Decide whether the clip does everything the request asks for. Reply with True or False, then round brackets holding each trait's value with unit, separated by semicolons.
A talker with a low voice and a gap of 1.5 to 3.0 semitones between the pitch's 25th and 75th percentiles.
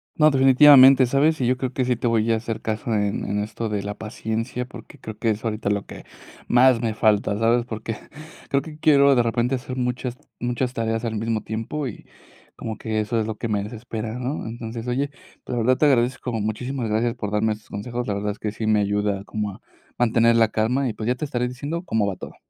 True (115 Hz; 2.7 semitones)